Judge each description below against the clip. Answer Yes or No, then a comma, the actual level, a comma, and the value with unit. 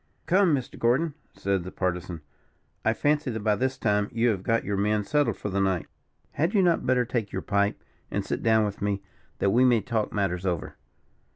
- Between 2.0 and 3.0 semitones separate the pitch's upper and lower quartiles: No, average, 4.3 semitones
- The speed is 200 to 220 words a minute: Yes, fast, 205 wpm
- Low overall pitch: Yes, low, 110 Hz